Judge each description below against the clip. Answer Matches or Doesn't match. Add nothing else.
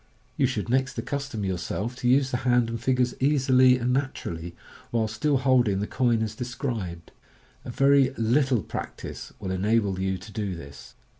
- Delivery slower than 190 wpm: Matches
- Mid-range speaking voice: Doesn't match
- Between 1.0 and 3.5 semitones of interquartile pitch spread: Doesn't match